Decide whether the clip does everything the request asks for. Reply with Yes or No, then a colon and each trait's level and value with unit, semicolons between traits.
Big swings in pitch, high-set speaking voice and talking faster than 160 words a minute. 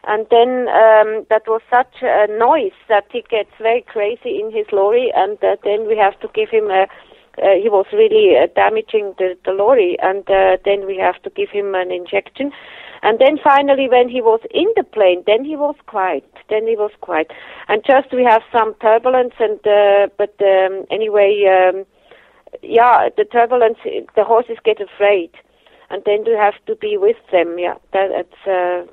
Yes: wide, 6.1 semitones; high, 220 Hz; average, 190 wpm